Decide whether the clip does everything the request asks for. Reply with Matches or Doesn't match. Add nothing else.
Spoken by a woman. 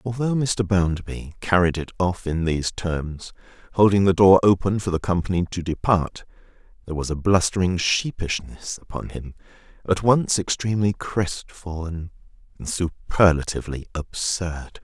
Doesn't match